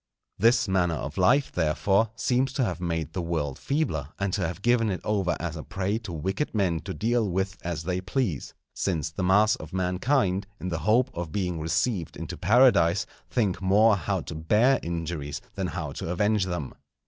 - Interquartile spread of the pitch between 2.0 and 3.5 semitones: No, average, 4.4 semitones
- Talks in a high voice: No, very low, 95 Hz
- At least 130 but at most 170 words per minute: No, average, 190 wpm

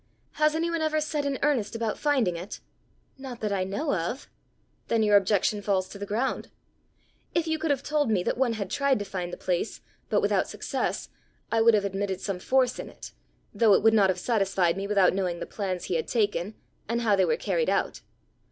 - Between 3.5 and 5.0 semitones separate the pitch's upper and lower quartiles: No, wide, 5.5 semitones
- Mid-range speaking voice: No, high, 215 Hz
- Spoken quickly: Yes, fast, 215 wpm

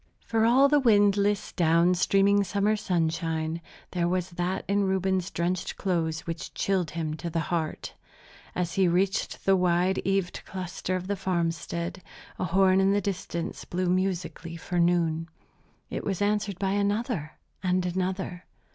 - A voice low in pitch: No, medium, 185 Hz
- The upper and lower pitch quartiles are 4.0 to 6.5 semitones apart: No, narrow, 2.4 semitones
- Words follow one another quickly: No, average, 150 wpm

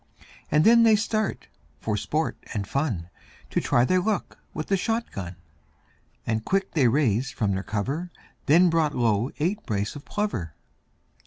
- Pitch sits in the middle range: Yes, medium, 145 Hz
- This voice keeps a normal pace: Yes, average, 160 wpm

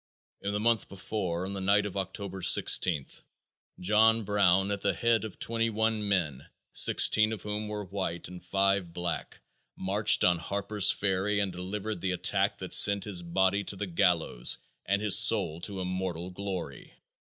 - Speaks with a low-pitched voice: Yes, low, 100 Hz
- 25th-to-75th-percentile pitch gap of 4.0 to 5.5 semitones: No, narrow, 2.4 semitones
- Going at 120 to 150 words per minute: No, average, 165 wpm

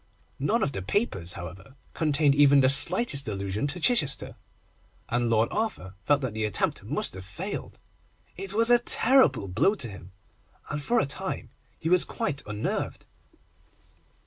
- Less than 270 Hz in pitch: Yes, medium, 140 Hz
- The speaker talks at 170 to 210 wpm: No, average, 155 wpm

